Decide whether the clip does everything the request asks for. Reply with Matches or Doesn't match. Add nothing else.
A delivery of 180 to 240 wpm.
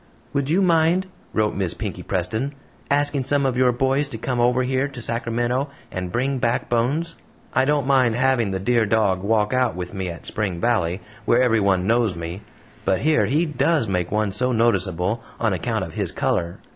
Matches